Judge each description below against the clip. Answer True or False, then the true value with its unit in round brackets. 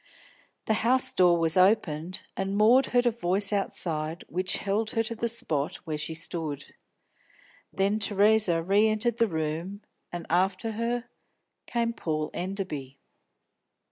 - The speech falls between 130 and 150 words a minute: True (140 wpm)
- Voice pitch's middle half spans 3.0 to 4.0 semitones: False (4.9 semitones)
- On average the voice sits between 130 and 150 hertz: False (195 Hz)